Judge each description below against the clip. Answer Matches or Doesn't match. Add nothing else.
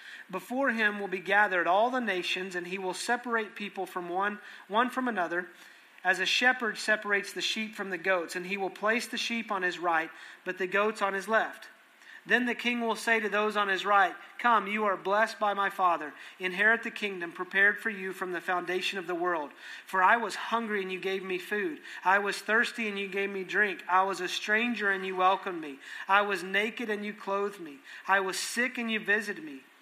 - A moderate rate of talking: Doesn't match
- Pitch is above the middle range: Matches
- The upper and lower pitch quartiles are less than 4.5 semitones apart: Matches